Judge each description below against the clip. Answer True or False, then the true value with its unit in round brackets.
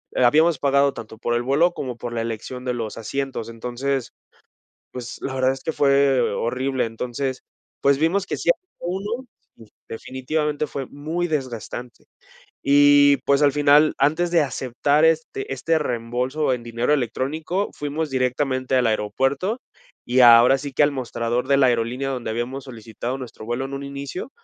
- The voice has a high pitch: False (135 Hz)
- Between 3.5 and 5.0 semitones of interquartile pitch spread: False (3.1 semitones)